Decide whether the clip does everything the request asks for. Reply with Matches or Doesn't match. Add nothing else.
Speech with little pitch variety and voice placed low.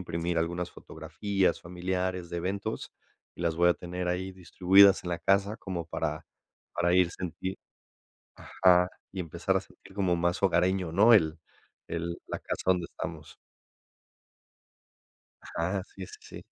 Matches